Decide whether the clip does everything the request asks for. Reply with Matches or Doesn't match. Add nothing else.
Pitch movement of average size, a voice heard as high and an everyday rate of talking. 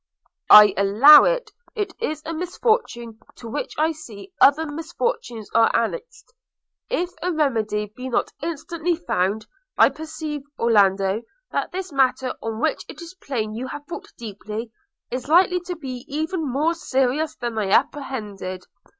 Doesn't match